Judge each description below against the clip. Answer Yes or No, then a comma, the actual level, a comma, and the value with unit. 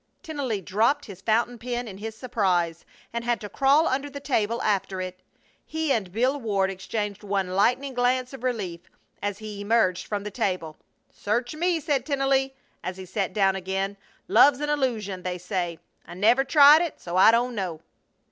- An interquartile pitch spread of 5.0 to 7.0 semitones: Yes, wide, 5.4 semitones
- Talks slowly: No, average, 180 wpm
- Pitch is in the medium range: No, high, 220 Hz